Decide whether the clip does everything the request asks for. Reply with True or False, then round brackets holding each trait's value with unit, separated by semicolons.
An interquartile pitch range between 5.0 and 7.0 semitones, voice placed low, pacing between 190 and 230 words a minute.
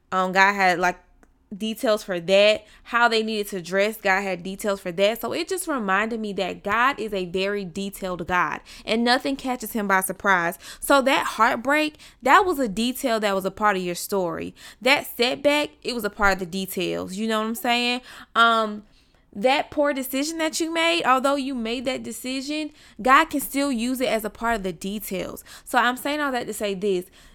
False (5.3 semitones; 220 Hz; 205 wpm)